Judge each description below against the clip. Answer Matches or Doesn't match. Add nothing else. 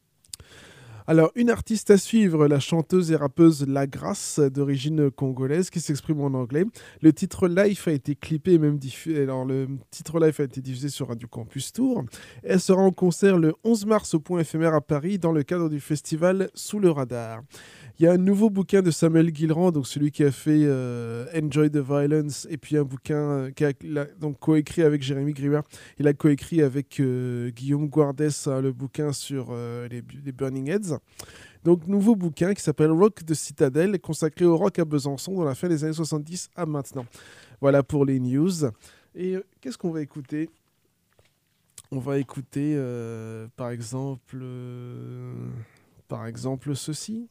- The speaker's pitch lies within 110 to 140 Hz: Doesn't match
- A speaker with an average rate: Matches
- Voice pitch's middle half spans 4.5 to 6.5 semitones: Doesn't match